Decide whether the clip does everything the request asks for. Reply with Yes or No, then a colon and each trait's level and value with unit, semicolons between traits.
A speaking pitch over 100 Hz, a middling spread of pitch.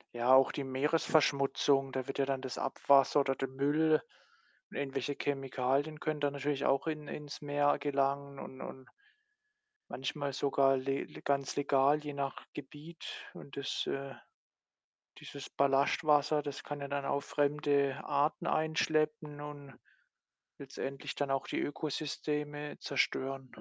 No: medium, 140 Hz; narrow, 1.3 semitones